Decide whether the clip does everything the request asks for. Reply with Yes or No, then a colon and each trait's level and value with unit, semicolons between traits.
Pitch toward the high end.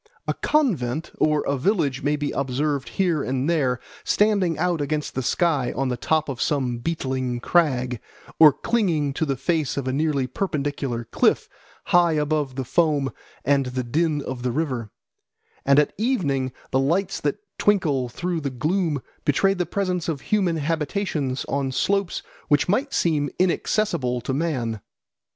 No: medium, 145 Hz